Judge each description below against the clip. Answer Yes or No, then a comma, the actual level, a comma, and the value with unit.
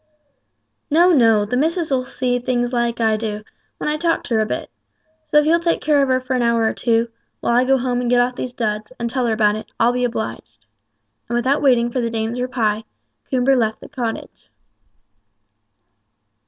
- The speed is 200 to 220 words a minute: Yes, fast, 205 wpm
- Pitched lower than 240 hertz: No, high, 245 Hz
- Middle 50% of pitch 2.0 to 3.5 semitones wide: Yes, narrow, 2.4 semitones